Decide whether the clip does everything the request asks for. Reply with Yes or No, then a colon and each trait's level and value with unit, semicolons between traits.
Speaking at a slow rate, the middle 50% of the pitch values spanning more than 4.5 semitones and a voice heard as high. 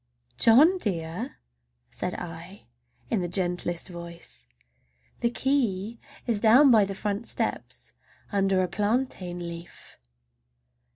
Yes: slow, 110 wpm; average, 4.9 semitones; high, 200 Hz